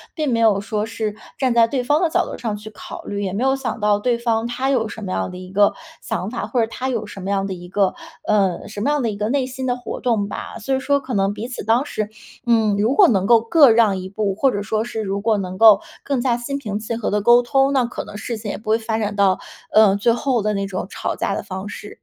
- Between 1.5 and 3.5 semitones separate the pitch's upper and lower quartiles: Yes, average, 3.2 semitones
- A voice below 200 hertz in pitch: No, high, 220 Hz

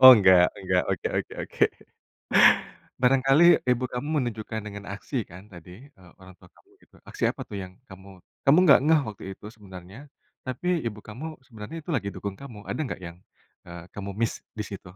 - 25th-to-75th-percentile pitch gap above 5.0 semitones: Yes, wide, 5.4 semitones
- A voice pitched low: Yes, low, 105 Hz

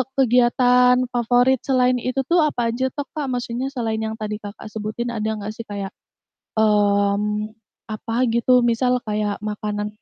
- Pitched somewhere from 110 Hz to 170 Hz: No, high, 230 Hz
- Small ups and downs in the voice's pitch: No, average, 3.0 semitones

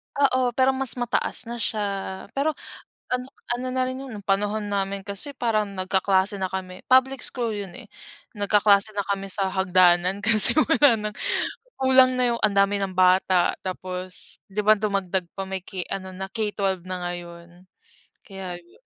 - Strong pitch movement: No, average, 4.0 semitones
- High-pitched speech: Yes, high, 200 Hz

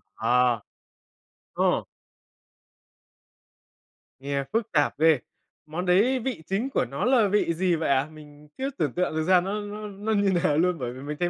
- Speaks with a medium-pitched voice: Yes, medium, 175 Hz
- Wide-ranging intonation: Yes, wide, 5.7 semitones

